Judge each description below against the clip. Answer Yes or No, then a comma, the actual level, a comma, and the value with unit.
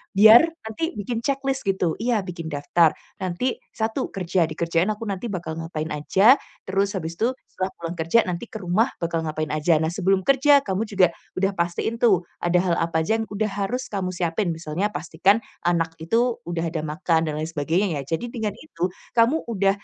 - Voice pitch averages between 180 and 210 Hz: Yes, medium, 185 Hz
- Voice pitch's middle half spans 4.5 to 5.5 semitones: Yes, average, 4.8 semitones